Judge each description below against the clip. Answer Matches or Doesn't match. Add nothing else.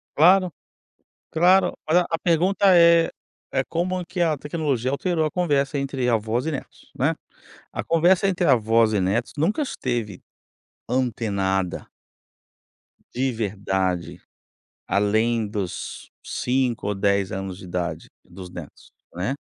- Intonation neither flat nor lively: Doesn't match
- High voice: Doesn't match